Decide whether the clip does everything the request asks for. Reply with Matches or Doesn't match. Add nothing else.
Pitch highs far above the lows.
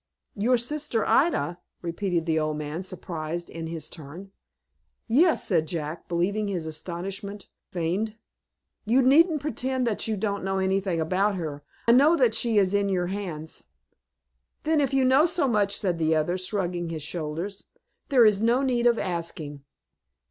Matches